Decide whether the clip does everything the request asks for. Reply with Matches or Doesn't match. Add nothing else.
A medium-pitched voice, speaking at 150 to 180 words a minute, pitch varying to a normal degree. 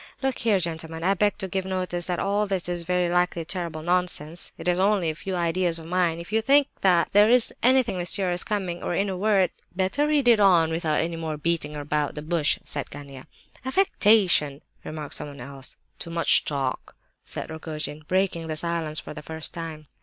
Doesn't match